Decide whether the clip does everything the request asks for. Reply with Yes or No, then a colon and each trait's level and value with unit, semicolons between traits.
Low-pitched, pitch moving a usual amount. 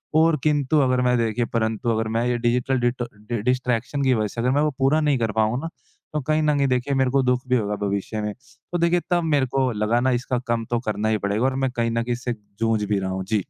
Yes: low, 125 Hz; average, 3.1 semitones